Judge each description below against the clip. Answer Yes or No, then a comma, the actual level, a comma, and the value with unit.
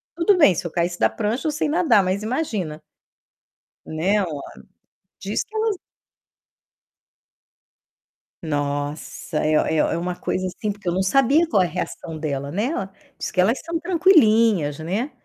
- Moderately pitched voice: No, high, 195 Hz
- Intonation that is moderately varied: No, wide, 8.8 semitones